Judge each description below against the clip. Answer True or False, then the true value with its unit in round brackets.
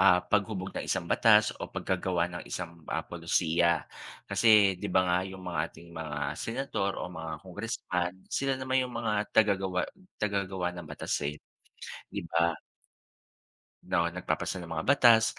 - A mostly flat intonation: False (3.7 semitones)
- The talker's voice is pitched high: False (90 Hz)